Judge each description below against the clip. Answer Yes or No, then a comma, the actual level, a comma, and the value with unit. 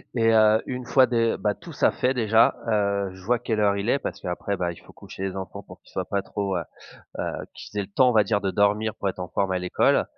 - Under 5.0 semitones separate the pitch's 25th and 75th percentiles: Yes, average, 2.8 semitones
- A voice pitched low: Yes, low, 105 Hz